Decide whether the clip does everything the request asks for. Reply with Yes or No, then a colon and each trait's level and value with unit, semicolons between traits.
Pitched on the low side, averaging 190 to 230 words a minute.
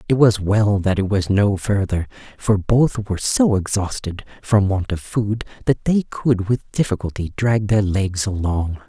No: low, 100 Hz; average, 175 wpm